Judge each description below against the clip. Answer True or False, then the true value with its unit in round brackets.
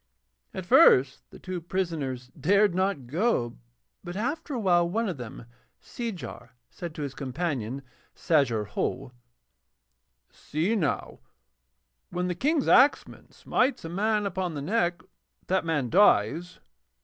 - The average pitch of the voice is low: False (175 Hz)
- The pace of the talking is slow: True (130 wpm)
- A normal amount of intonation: False (6.3 semitones)